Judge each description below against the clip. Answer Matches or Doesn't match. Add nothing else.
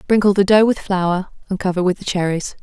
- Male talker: Doesn't match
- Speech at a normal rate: Doesn't match